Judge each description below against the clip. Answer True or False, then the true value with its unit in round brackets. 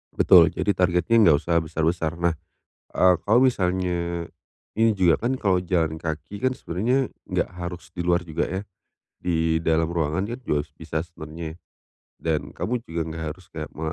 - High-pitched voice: False (85 Hz)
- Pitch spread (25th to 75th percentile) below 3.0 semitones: True (2.4 semitones)